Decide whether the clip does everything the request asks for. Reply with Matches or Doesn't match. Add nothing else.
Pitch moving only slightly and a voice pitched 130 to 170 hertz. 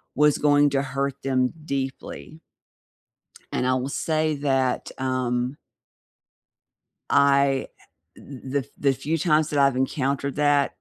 Matches